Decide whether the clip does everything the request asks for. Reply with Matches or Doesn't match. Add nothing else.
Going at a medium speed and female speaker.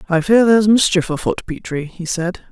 Matches